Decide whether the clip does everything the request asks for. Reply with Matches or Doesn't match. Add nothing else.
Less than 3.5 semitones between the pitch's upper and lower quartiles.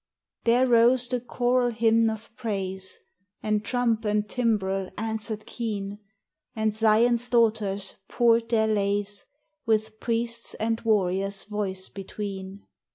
Matches